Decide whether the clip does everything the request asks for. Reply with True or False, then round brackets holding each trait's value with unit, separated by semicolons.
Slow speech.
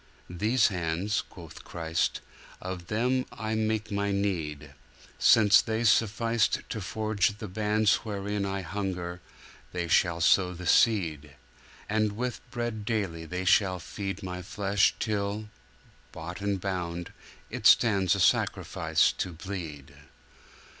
True (125 wpm)